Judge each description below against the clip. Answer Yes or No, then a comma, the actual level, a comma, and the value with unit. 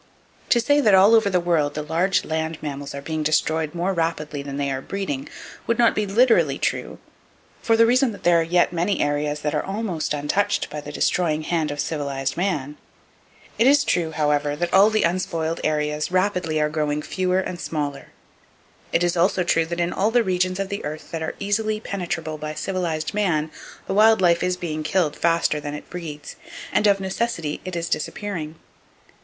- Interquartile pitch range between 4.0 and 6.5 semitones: Yes, average, 4.3 semitones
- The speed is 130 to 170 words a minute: No, average, 195 wpm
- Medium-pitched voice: Yes, medium, 170 Hz